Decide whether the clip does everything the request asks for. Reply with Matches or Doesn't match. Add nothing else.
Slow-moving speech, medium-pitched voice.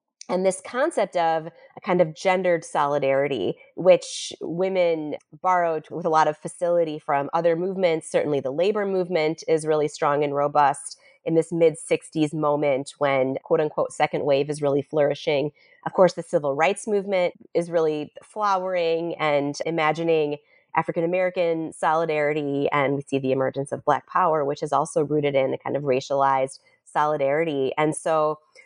Doesn't match